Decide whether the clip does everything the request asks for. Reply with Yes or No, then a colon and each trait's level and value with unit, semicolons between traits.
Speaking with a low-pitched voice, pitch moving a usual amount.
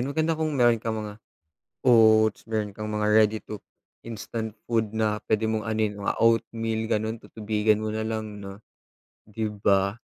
No: low, 110 Hz; narrow, 1.0 semitones